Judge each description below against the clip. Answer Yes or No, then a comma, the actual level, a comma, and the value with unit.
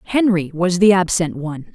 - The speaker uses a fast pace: No, average, 170 wpm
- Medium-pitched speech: Yes, medium, 180 Hz